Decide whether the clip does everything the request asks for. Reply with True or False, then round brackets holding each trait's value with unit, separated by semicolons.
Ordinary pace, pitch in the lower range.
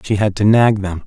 False (280 wpm; 100 Hz)